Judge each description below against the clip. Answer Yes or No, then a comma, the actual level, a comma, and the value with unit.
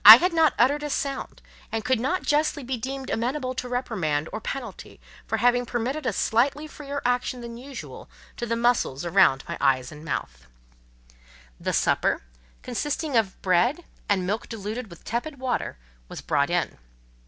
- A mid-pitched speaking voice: No, high, 245 Hz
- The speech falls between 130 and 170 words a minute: Yes, average, 165 wpm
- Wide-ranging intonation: No, average, 4.5 semitones